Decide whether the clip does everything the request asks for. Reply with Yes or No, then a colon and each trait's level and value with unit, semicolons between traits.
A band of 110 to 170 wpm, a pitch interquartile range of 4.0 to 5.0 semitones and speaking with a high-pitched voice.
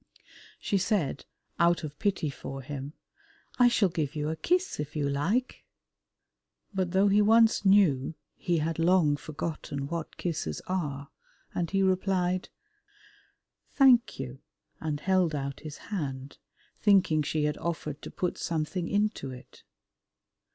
No: slow, 135 wpm; average, 4.7 semitones; medium, 165 Hz